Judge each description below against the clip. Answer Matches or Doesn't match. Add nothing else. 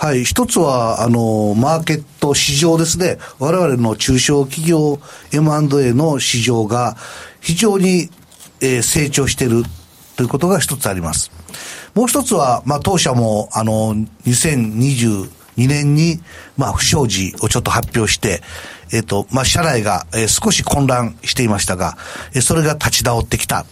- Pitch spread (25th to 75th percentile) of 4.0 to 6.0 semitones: Matches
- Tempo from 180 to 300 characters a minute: Matches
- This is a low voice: Matches